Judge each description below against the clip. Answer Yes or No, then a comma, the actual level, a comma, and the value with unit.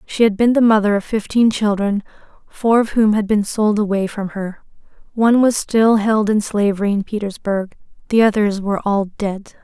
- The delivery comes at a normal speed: Yes, average, 185 wpm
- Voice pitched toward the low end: No, high, 210 Hz